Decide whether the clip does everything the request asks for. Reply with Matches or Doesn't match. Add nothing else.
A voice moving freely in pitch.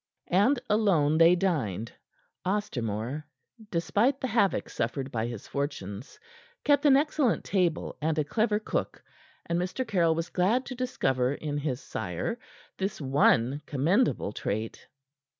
Matches